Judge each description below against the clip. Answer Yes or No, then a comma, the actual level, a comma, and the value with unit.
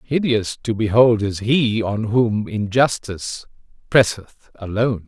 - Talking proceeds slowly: Yes, slow, 120 wpm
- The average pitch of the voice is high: No, low, 110 Hz